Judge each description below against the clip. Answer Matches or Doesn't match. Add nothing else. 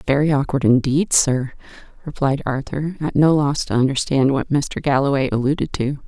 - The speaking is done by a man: Doesn't match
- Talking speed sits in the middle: Matches